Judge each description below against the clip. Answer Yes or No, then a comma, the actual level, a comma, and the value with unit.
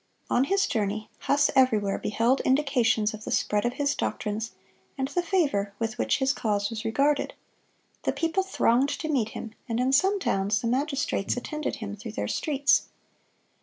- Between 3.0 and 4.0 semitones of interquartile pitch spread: No, average, 5.0 semitones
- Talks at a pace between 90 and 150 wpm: No, average, 175 wpm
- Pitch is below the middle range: No, high, 245 Hz